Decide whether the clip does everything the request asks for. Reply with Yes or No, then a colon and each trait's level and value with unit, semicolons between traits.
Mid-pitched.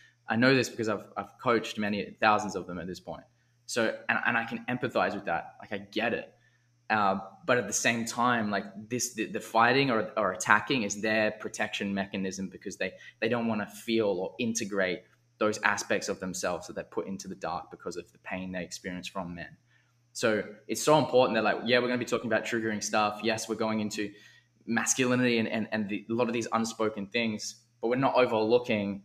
No: low, 110 Hz